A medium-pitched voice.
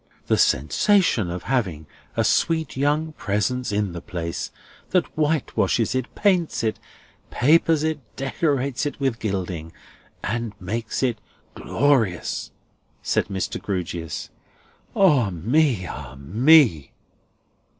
No: low, 120 Hz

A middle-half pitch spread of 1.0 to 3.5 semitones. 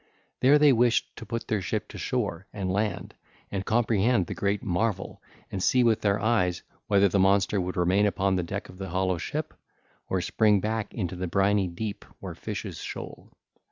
Yes: average, 3.0 semitones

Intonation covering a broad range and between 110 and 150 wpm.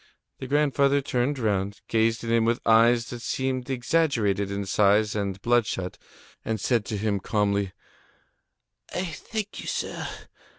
No: average, 4.3 semitones; average, 140 wpm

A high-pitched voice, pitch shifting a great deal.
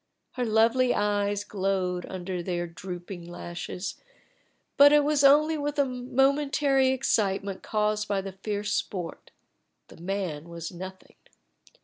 Yes: high, 205 Hz; wide, 6.2 semitones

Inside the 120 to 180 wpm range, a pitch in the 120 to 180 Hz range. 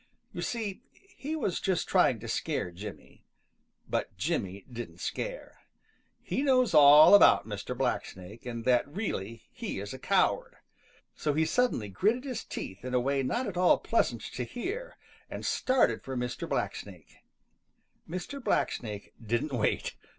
Yes: average, 150 wpm; medium, 140 Hz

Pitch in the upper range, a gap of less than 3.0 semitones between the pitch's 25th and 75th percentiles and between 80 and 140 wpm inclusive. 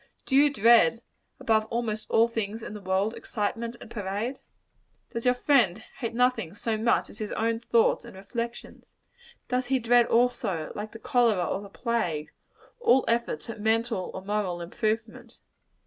No: high, 225 Hz; narrow, 2.5 semitones; average, 165 wpm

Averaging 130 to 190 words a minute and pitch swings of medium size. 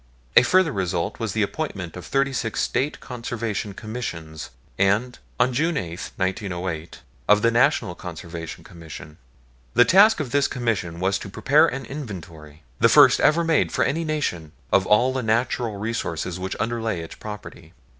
No: average, 160 wpm; wide, 6.3 semitones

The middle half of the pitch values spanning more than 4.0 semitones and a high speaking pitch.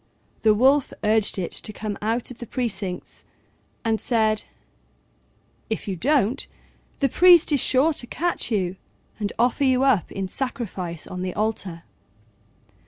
Yes: average, 4.7 semitones; high, 220 Hz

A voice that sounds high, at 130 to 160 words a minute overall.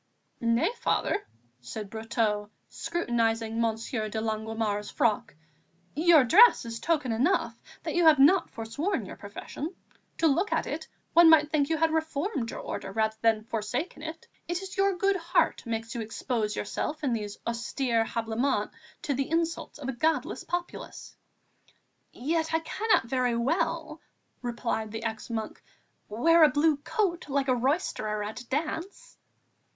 Yes: very high, 260 Hz; average, 155 wpm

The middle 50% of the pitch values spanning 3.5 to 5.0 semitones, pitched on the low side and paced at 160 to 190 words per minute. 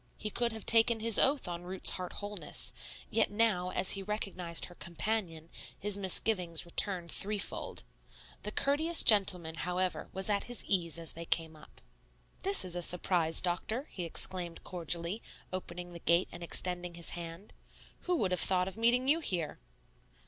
No: average, 3.8 semitones; medium, 185 Hz; average, 165 wpm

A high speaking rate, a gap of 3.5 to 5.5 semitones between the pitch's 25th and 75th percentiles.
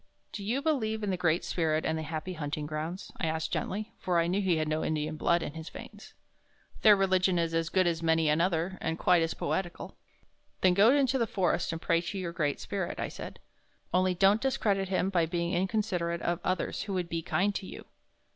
No: fast, 215 wpm; average, 3.0 semitones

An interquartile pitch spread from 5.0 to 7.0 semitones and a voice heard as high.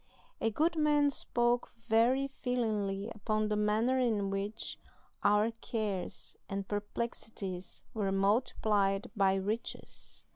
No: average, 3.2 semitones; high, 215 Hz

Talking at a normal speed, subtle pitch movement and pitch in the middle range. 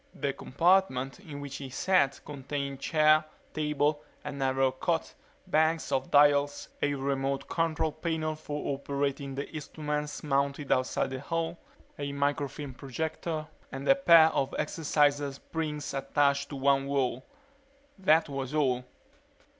No: slow, 130 wpm; narrow, 2.2 semitones; medium, 145 Hz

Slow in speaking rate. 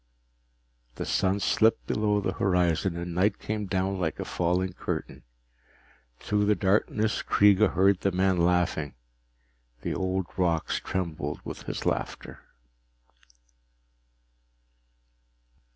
Yes: slow, 110 wpm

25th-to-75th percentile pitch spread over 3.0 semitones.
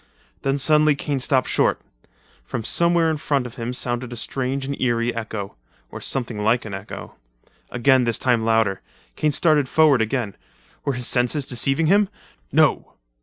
Yes: average, 3.6 semitones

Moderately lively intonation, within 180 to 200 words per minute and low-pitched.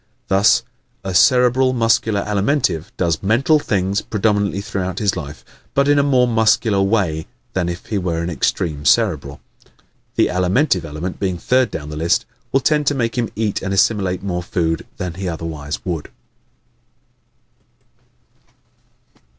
No: average, 5.0 semitones; average, 145 wpm; very low, 95 Hz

